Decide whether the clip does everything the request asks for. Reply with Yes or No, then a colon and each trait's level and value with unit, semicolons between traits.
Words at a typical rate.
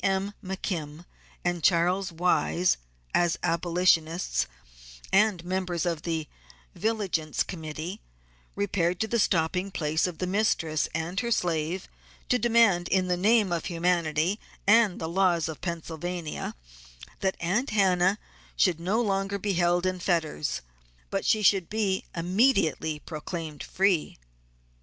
No: slow, 130 wpm